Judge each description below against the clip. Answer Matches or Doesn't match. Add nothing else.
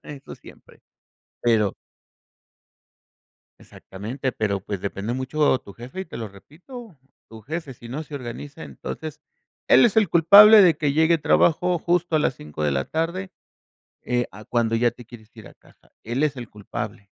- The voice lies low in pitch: Matches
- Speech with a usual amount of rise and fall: Doesn't match